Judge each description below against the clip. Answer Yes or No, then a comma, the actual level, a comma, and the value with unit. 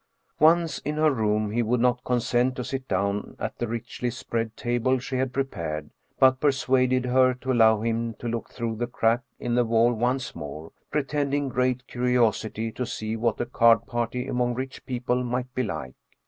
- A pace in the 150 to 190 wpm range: Yes, average, 185 wpm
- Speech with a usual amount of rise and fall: No, narrow, 2.3 semitones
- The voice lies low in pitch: Yes, low, 120 Hz